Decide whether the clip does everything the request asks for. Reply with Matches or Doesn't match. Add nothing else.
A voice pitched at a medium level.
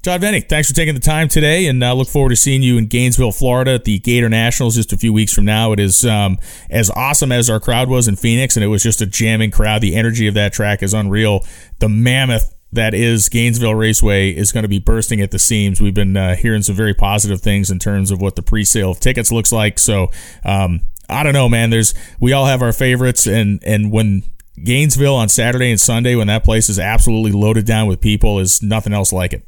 Doesn't match